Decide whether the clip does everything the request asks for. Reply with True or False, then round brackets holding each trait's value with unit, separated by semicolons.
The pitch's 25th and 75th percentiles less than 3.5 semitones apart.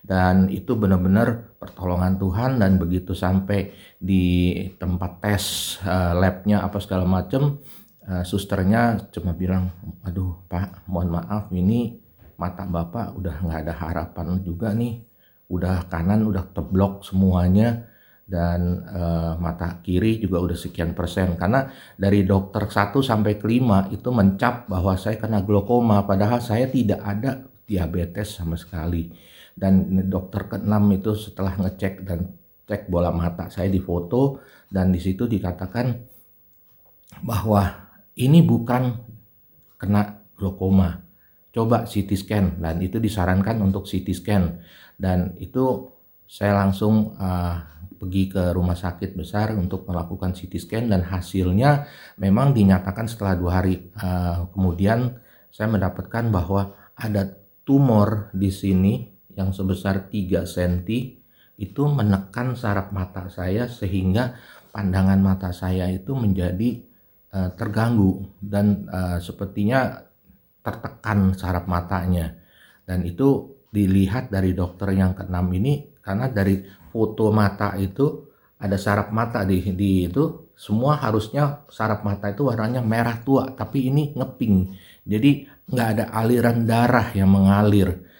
True (2.9 semitones)